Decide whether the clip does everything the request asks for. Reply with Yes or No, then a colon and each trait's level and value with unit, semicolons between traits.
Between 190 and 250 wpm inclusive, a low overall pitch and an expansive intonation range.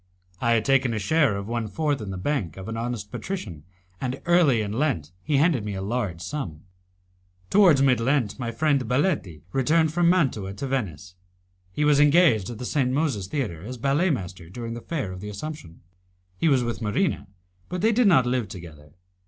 Yes: average, 195 wpm; low, 125 Hz; wide, 6.9 semitones